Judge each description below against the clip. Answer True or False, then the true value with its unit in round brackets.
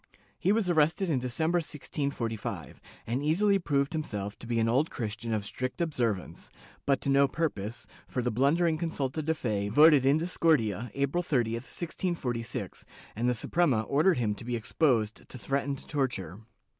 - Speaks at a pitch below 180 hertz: True (135 Hz)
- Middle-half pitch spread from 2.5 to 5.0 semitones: False (5.6 semitones)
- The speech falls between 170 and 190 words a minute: False (160 wpm)